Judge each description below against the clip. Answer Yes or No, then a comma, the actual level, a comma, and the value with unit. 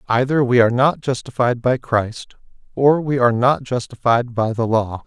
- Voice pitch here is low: Yes, low, 125 Hz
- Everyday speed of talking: Yes, average, 180 wpm